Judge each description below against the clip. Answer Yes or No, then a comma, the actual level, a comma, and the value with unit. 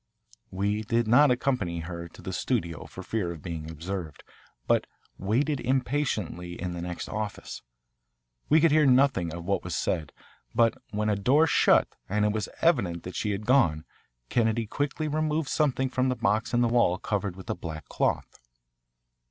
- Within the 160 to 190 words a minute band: Yes, average, 175 wpm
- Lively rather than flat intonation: Yes, wide, 6.6 semitones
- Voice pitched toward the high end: No, low, 105 Hz